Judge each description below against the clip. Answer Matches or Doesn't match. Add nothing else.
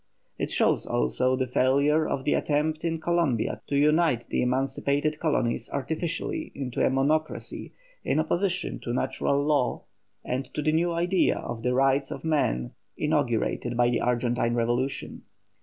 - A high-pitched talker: Doesn't match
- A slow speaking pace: Doesn't match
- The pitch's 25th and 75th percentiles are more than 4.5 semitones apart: Doesn't match